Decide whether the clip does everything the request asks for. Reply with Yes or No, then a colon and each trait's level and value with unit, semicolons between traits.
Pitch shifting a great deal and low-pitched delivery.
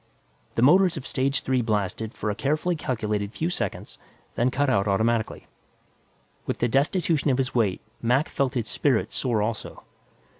No: average, 4.3 semitones; low, 125 Hz